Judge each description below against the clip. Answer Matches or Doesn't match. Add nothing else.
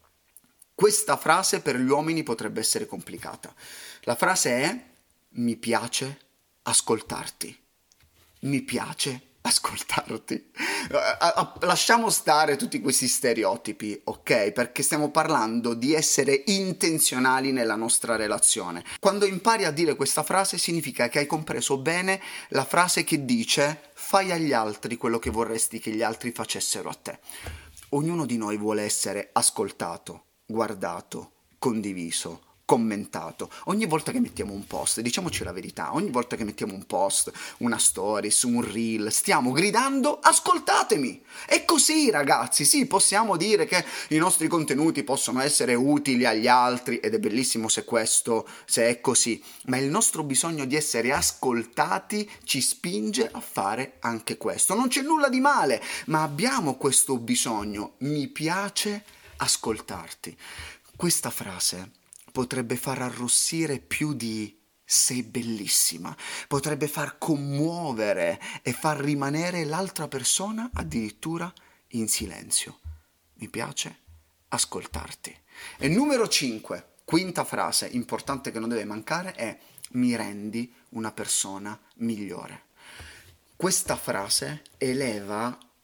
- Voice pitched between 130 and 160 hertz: Matches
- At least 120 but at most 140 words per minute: Matches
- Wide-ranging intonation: Matches